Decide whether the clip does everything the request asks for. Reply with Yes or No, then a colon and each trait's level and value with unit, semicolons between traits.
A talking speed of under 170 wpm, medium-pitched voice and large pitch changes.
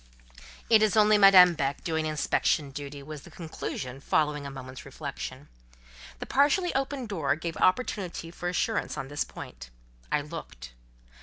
Yes: average, 150 wpm; medium, 160 Hz; wide, 5.9 semitones